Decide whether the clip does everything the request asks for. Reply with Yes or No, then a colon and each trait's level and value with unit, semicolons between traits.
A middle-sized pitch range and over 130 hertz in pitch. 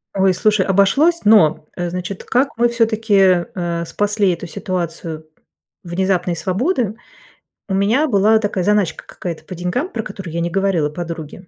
Yes: average, 3.6 semitones; high, 190 Hz